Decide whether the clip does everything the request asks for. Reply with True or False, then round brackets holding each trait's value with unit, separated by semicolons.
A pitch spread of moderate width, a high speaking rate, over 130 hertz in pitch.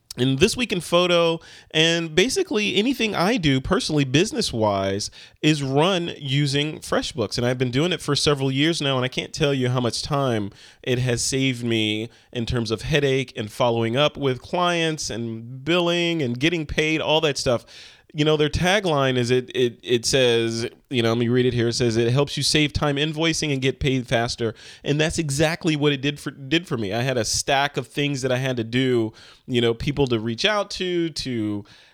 True (4.6 semitones; 210 wpm; 140 Hz)